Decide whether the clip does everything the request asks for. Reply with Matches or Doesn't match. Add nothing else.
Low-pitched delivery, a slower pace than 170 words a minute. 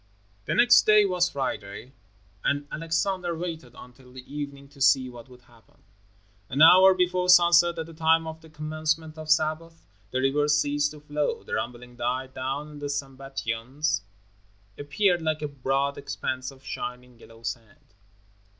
Doesn't match